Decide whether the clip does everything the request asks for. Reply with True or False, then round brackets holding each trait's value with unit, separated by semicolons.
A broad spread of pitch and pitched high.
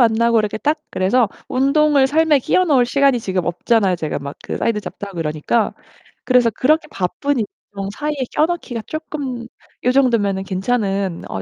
True (6.0 semitones; 235 Hz)